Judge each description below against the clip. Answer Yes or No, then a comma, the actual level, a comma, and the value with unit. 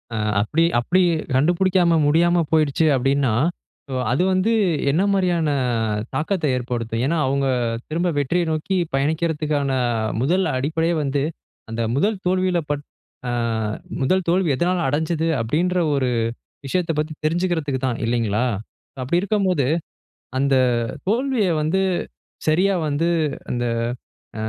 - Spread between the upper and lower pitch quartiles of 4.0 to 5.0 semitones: Yes, average, 4.6 semitones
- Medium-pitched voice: Yes, medium, 160 Hz